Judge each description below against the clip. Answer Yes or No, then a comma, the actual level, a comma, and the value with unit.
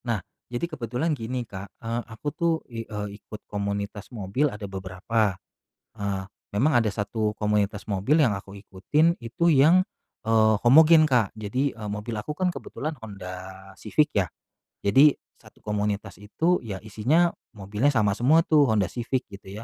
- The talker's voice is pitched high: No, low, 110 Hz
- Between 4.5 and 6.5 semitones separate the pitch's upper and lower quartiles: Yes, average, 5.1 semitones